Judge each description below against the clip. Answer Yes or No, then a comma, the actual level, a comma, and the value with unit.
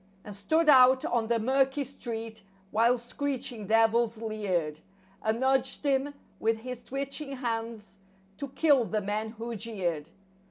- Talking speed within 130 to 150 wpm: Yes, slow, 135 wpm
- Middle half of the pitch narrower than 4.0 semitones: Yes, average, 3.4 semitones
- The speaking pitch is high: Yes, high, 230 Hz